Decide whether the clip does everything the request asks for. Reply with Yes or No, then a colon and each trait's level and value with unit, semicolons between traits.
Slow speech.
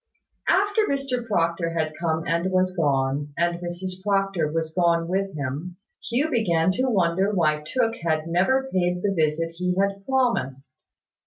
No: average, 155 wpm